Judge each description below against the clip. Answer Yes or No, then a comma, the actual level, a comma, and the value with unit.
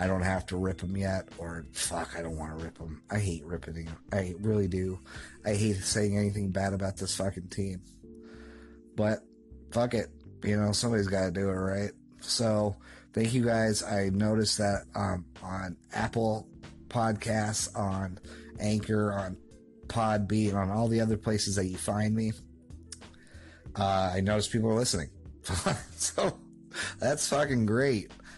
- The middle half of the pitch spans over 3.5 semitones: Yes, average, 4.0 semitones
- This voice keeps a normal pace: Yes, average, 160 wpm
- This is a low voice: Yes, low, 100 Hz